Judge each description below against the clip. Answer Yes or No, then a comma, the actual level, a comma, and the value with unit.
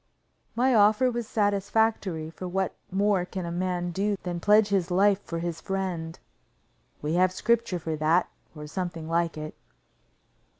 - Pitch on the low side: No, medium, 185 Hz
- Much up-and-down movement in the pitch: No, average, 3.3 semitones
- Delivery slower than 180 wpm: Yes, average, 155 wpm